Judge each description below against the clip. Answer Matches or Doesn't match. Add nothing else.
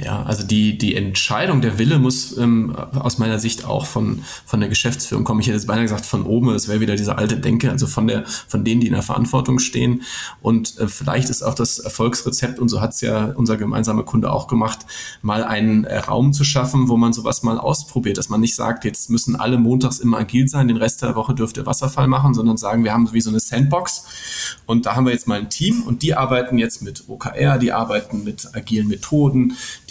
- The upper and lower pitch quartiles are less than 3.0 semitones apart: Matches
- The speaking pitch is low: Matches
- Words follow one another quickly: Matches